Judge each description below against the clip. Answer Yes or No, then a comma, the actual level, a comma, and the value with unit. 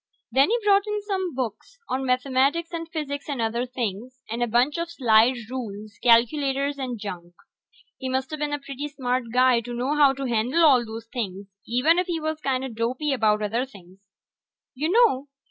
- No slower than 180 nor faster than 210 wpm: Yes, average, 185 wpm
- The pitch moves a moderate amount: Yes, average, 4.1 semitones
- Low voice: No, very high, 260 Hz